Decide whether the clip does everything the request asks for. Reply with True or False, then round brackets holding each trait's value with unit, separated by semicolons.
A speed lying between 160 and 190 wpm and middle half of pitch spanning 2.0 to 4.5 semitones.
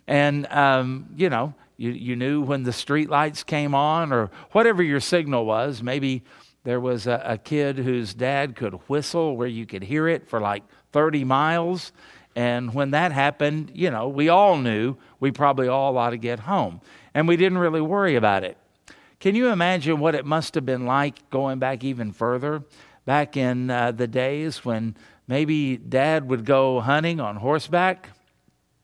True (175 wpm; 3.7 semitones)